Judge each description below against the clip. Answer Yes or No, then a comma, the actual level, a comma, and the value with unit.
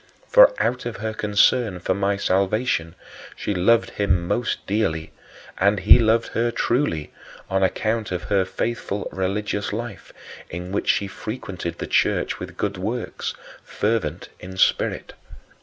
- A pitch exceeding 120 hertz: No, low, 100 Hz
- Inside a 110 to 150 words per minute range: Yes, average, 140 wpm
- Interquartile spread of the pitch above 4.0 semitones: No, average, 3.4 semitones